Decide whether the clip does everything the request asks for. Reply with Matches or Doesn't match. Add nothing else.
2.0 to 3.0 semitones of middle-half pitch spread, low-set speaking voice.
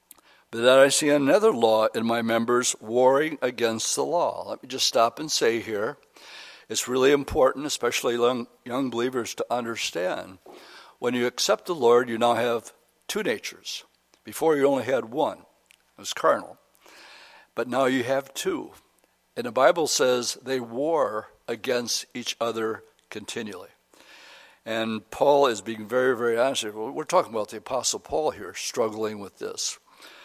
Matches